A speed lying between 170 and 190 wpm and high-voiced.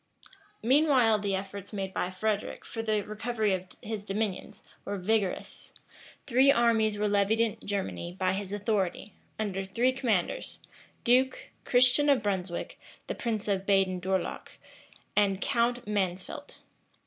No: slow, 135 wpm; high, 210 Hz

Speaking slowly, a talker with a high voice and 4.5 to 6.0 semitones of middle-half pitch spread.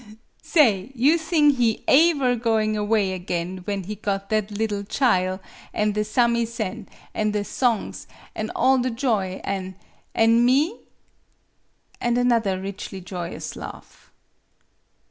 No: slow, 130 wpm; high, 215 Hz; average, 3.9 semitones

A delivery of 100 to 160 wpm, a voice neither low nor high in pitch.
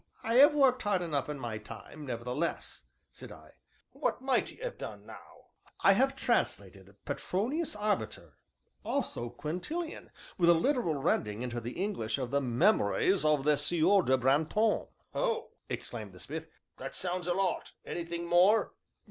Yes: average, 155 wpm; medium, 170 Hz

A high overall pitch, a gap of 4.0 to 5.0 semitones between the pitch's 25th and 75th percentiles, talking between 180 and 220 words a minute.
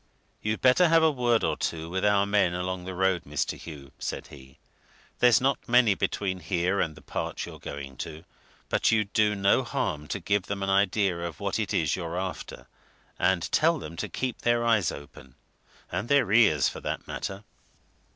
No: very low, 95 Hz; average, 4.7 semitones; average, 190 wpm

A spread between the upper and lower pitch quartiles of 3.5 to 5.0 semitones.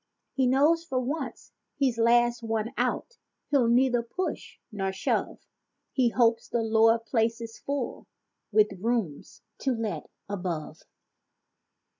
No: narrow, 2.5 semitones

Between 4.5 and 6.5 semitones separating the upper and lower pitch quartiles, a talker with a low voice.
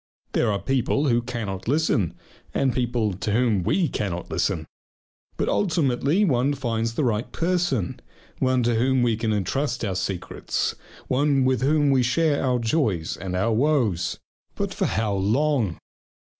Yes: average, 4.8 semitones; low, 120 Hz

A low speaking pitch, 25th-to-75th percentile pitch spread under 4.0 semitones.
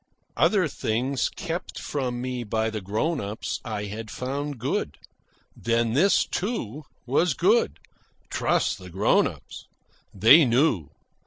No: low, 125 Hz; average, 5.3 semitones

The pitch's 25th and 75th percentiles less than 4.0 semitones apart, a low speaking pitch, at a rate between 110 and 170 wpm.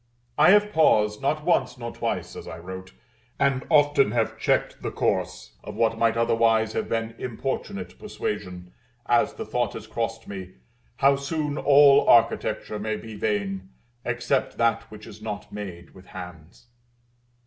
No: average, 4.6 semitones; low, 115 Hz; average, 155 wpm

